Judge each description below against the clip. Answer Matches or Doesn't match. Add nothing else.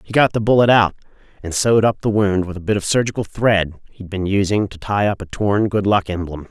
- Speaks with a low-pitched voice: Matches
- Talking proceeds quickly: Matches